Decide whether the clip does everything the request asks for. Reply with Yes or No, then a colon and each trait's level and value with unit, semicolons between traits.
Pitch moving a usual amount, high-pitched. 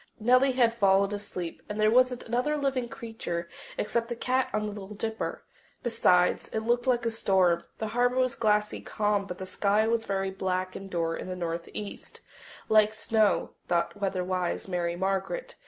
Yes: average, 3.9 semitones; high, 210 Hz